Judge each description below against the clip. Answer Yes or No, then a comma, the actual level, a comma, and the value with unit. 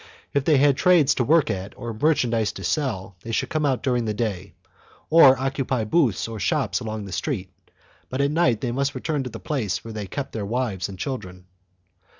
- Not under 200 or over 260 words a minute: Yes, fast, 205 wpm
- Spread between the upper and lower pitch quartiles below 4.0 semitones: No, average, 5.1 semitones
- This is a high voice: No, low, 120 Hz